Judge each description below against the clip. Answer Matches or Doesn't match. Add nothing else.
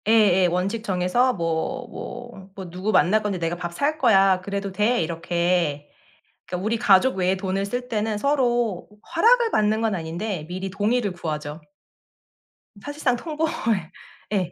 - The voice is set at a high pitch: Matches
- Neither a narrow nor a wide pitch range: Matches